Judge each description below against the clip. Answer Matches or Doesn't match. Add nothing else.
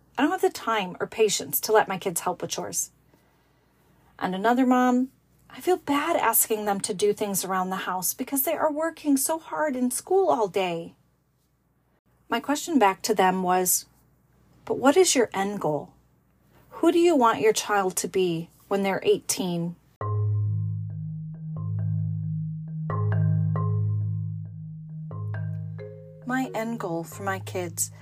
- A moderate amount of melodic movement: Doesn't match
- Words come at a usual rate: Matches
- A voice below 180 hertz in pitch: Doesn't match